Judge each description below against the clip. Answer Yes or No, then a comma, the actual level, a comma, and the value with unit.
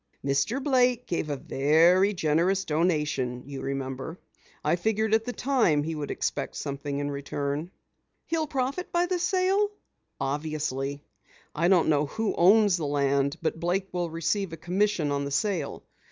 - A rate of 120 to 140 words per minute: No, average, 155 wpm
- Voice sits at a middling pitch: Yes, medium, 165 Hz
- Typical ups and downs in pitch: No, wide, 6.8 semitones